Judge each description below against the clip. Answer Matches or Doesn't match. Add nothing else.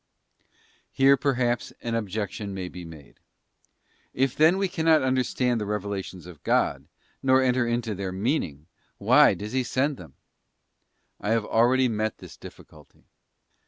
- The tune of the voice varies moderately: Matches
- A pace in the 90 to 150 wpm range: Matches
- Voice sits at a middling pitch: Doesn't match